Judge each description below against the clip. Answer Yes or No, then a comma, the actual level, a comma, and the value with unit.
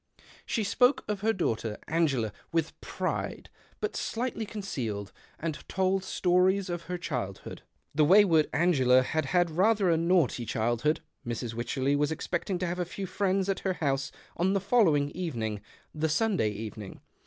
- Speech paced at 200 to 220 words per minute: No, average, 165 wpm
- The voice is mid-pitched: Yes, medium, 165 Hz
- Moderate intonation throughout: No, wide, 6.5 semitones